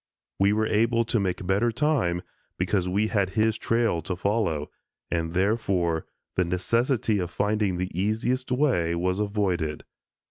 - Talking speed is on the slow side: No, average, 145 wpm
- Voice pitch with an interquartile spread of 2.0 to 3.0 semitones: No, average, 3.9 semitones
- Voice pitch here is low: Yes, low, 100 Hz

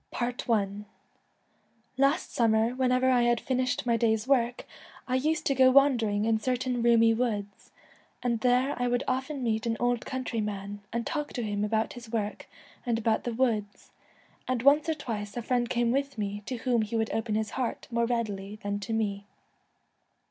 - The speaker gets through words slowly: No, average, 175 wpm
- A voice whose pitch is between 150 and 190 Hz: No, high, 235 Hz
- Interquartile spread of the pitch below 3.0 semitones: Yes, narrow, 2.6 semitones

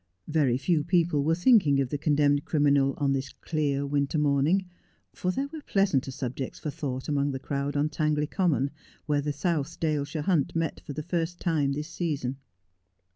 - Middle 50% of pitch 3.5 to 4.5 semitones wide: No, average, 2.8 semitones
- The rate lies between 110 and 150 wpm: No, average, 180 wpm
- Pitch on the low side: No, medium, 145 Hz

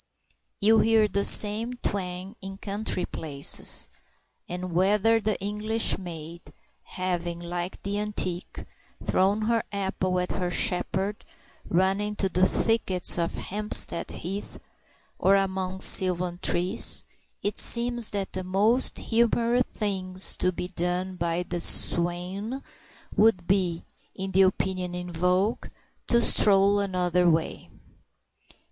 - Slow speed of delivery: Yes, slow, 120 wpm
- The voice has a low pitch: No, high, 190 Hz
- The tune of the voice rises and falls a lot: No, narrow, 2.6 semitones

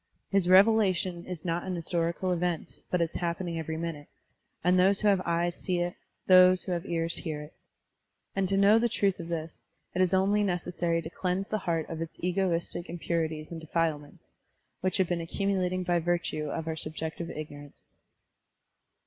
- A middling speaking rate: Yes, average, 180 wpm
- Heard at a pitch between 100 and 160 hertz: No, medium, 175 Hz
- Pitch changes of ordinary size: No, narrow, 2.0 semitones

